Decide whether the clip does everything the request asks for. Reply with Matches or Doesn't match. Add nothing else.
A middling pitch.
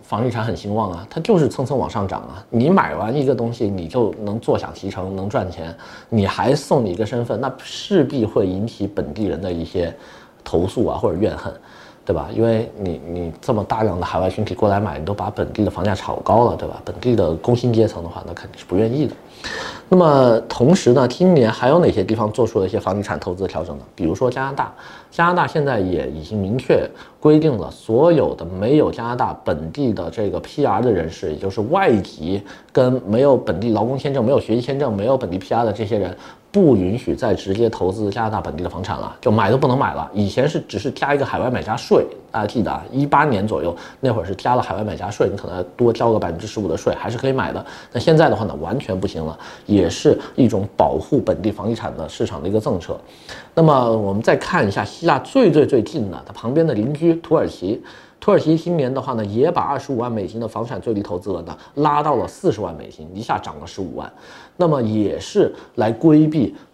Doesn't match